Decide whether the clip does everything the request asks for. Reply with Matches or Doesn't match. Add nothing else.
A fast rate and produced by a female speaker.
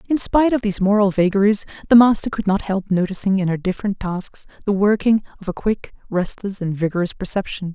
Doesn't match